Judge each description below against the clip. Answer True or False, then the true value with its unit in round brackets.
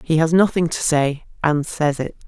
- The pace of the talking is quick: True (210 wpm)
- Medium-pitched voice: True (155 Hz)